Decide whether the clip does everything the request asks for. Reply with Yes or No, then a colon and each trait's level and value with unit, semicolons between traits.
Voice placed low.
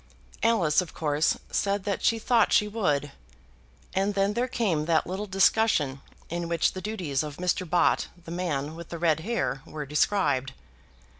No: medium, 175 Hz